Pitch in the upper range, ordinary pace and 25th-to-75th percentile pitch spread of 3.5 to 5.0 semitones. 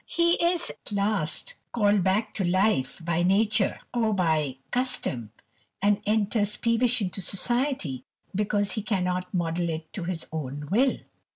Yes: high, 200 Hz; average, 145 wpm; average, 4.5 semitones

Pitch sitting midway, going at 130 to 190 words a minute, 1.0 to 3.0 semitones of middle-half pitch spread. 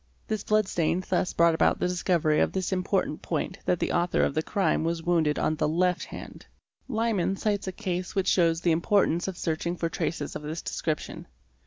No: medium, 175 Hz; average, 200 wpm; narrow, 2.6 semitones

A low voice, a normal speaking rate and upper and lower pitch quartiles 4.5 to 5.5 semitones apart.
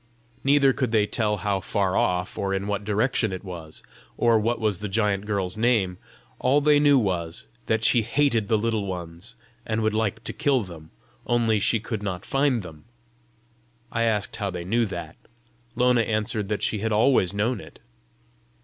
No: low, 105 Hz; average, 180 wpm; average, 3.3 semitones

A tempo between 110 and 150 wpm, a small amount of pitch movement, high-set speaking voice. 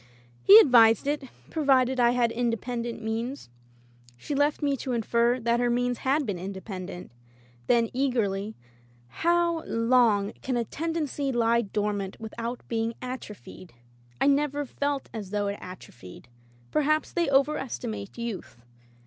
No: average, 145 wpm; average, 4.6 semitones; high, 235 Hz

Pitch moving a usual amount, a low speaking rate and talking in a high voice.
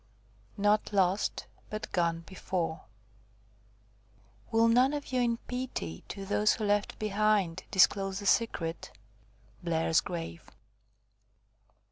Yes: average, 3.9 semitones; slow, 105 wpm; high, 200 Hz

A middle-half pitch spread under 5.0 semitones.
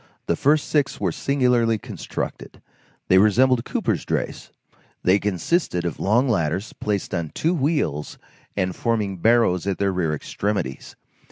No: wide, 5.4 semitones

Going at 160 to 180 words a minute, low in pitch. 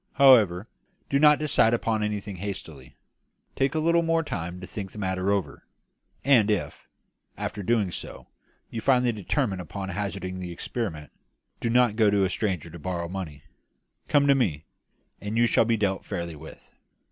Yes: average, 170 wpm; low, 100 Hz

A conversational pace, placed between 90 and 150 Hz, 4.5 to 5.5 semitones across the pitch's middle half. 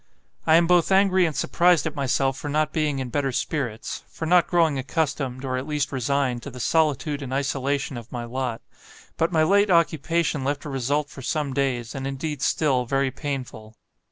No: average, 190 wpm; medium, 140 Hz; average, 3.2 semitones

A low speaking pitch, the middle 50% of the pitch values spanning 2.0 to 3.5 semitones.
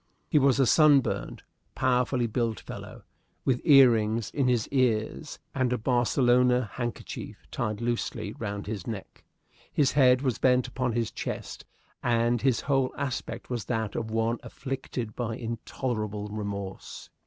Yes: low, 120 Hz; average, 2.7 semitones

